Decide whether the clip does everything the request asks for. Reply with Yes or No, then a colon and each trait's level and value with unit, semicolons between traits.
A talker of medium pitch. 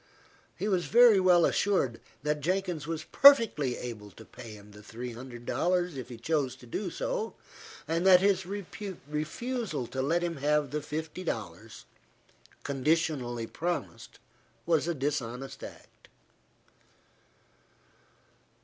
Yes: medium, 150 Hz